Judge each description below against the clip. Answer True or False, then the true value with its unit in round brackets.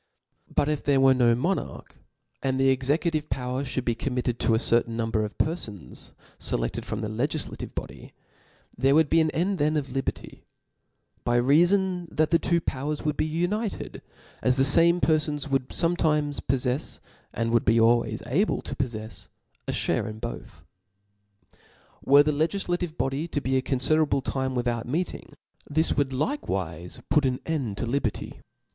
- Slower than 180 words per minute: True (170 wpm)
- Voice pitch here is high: False (135 Hz)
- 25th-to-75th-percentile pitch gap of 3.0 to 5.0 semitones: True (4.5 semitones)